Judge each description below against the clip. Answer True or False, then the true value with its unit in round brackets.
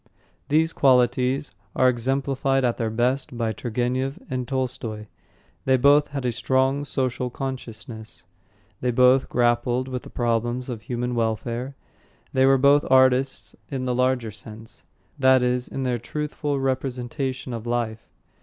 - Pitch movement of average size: False (1.9 semitones)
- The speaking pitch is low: True (125 Hz)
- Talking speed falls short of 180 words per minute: True (140 wpm)